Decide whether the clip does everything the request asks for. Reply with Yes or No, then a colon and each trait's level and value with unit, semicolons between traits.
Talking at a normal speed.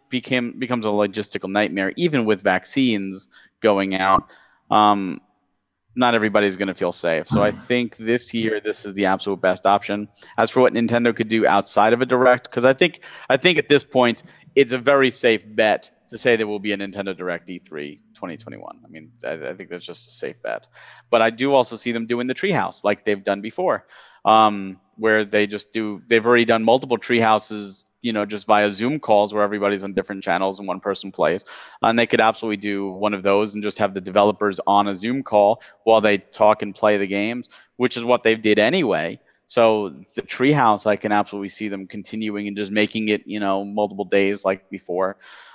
No: fast, 210 wpm